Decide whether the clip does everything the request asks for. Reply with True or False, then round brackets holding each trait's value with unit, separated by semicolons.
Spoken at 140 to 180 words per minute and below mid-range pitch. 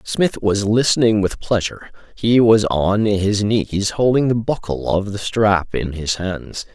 True (170 wpm; 105 Hz)